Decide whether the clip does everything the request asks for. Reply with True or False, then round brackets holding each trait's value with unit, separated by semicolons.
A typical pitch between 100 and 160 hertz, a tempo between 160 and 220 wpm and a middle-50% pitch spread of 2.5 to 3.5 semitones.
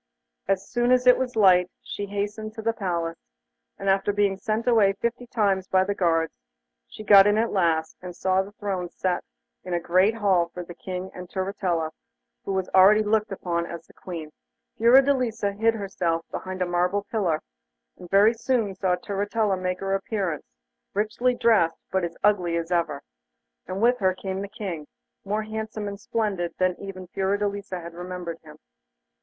False (195 Hz; 175 wpm; 3.1 semitones)